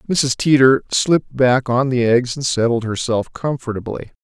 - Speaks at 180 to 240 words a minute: No, average, 155 wpm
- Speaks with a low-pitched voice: Yes, low, 125 Hz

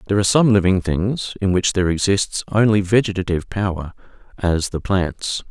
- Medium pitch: No, very low, 95 Hz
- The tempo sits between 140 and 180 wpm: Yes, average, 165 wpm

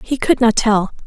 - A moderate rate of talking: No, fast, 225 wpm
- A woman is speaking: Yes, female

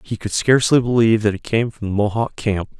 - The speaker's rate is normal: No, fast, 235 wpm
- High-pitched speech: No, low, 110 Hz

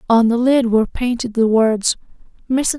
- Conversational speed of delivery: Yes, average, 150 wpm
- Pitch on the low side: No, high, 235 Hz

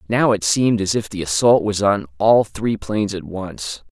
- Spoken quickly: Yes, fast, 215 wpm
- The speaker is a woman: No, male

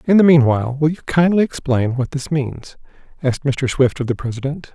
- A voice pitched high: No, medium, 140 Hz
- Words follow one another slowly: No, average, 200 wpm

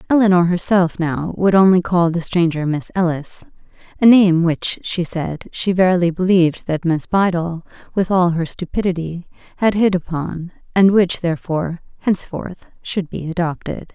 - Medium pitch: Yes, medium, 175 Hz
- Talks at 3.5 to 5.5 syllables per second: Yes, 4.8 syllables/s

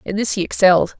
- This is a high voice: Yes, high, 195 Hz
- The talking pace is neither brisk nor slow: No, fast, 240 wpm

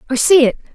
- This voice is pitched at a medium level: No, very high, 280 Hz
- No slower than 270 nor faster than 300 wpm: No, fast, 245 wpm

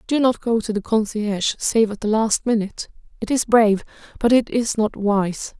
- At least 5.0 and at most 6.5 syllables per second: Yes, 5.1 syllables/s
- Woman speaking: Yes, female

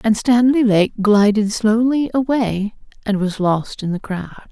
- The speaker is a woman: Yes, female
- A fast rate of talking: No, average, 160 wpm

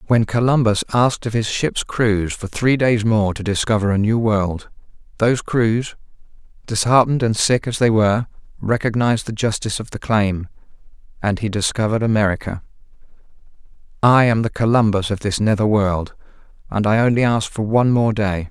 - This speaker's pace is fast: No, average, 160 wpm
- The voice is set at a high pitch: No, low, 110 Hz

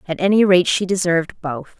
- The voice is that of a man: No, female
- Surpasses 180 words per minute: Yes, average, 200 wpm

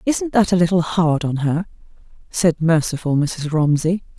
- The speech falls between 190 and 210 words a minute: No, average, 160 wpm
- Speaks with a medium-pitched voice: Yes, medium, 170 Hz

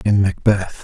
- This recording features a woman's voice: No, male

